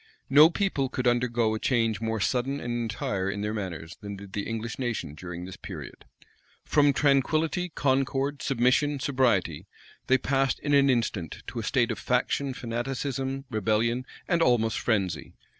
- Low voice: Yes, low, 120 Hz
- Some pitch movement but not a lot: Yes, average, 4.1 semitones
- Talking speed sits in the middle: Yes, average, 160 wpm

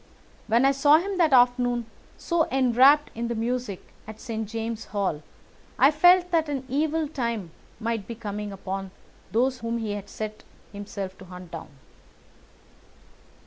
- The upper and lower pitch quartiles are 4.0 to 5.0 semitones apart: Yes, average, 4.7 semitones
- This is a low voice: No, high, 235 Hz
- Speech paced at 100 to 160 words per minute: Yes, average, 150 wpm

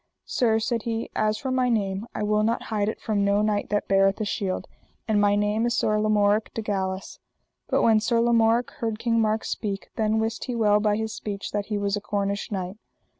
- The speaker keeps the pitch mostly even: Yes, narrow, 1.7 semitones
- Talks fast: Yes, fast, 220 wpm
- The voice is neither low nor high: No, high, 215 Hz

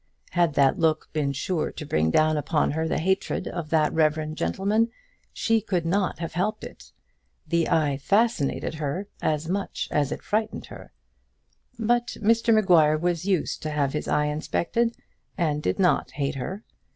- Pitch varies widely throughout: No, average, 4.6 semitones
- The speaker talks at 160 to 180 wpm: Yes, average, 165 wpm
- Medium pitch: Yes, medium, 165 Hz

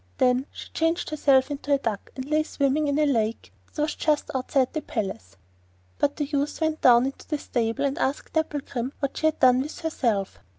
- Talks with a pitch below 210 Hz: No, very high, 275 Hz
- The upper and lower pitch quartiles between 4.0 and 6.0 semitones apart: No, average, 3.2 semitones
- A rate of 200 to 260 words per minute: Yes, fast, 205 wpm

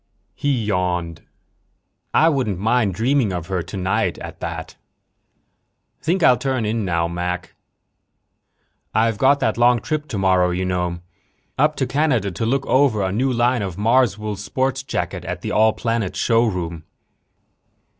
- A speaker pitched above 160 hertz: No, low, 110 Hz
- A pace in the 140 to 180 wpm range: Yes, average, 145 wpm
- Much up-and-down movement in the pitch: Yes, wide, 5.9 semitones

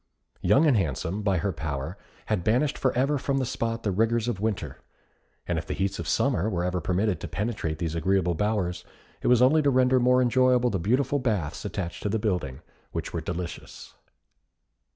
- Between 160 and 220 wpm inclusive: Yes, average, 195 wpm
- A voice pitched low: Yes, low, 105 Hz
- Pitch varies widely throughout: Yes, wide, 5.9 semitones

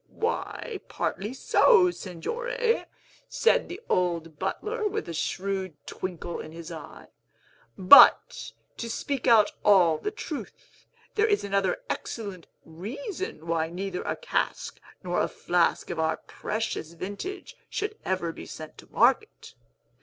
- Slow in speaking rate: Yes, slow, 130 wpm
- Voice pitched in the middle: No, high, 195 Hz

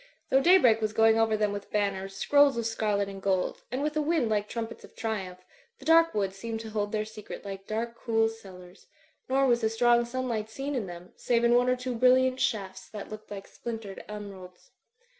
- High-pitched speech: Yes, high, 225 Hz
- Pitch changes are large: No, average, 3.3 semitones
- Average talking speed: No, fast, 215 wpm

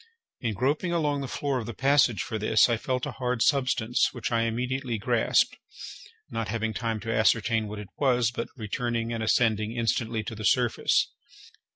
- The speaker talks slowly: No, average, 180 wpm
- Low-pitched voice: Yes, low, 115 Hz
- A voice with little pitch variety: Yes, narrow, 2.2 semitones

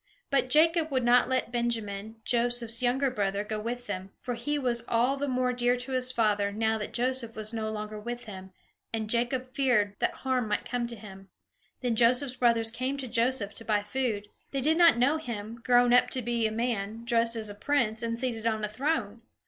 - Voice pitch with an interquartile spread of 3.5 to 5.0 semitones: No, narrow, 2.6 semitones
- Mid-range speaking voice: No, high, 235 Hz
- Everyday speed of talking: No, fast, 210 wpm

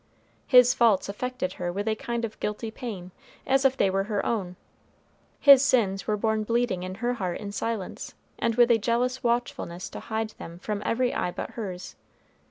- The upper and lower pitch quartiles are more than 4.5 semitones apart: No, average, 3.8 semitones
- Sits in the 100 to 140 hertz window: No, high, 220 Hz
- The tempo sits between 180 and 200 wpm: Yes, average, 185 wpm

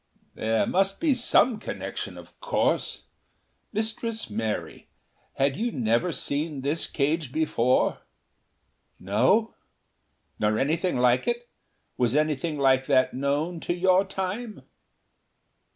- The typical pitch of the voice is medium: Yes, medium, 155 Hz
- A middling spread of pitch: No, wide, 7.1 semitones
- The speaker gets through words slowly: Yes, slow, 110 wpm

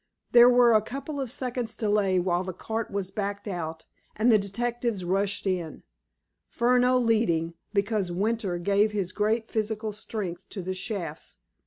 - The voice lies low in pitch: No, high, 210 Hz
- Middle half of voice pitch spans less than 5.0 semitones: Yes, average, 3.6 semitones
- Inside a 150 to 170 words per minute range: Yes, average, 155 wpm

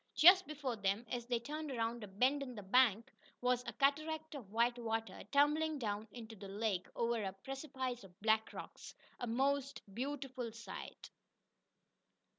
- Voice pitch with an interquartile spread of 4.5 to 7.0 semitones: No, average, 4.0 semitones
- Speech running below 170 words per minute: Yes, average, 160 wpm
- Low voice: No, high, 245 Hz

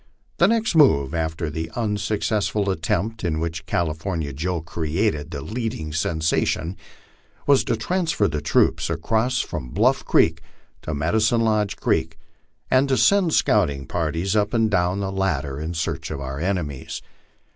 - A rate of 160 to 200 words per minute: No, average, 145 wpm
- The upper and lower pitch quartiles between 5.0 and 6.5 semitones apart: Yes, wide, 5.6 semitones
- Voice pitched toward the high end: No, very low, 90 Hz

